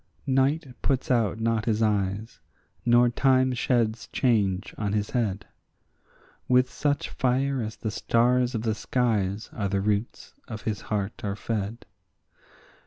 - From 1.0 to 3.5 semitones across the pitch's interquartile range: Yes, average, 3.2 semitones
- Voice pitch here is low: Yes, low, 115 Hz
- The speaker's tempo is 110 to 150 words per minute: Yes, average, 140 wpm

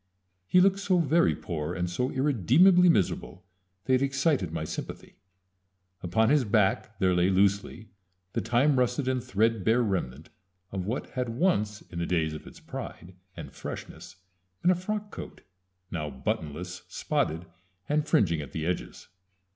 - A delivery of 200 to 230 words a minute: No, average, 155 wpm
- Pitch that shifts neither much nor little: No, wide, 7.5 semitones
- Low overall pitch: Yes, low, 110 Hz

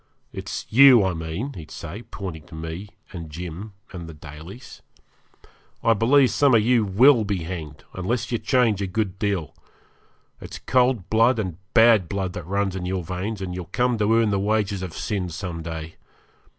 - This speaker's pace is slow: No, average, 180 wpm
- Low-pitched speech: Yes, low, 100 Hz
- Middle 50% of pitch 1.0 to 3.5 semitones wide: No, average, 4.4 semitones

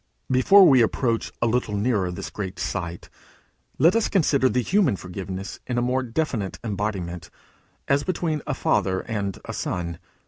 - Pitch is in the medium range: No, low, 115 Hz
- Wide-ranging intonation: Yes, wide, 6.1 semitones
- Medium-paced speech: Yes, average, 165 wpm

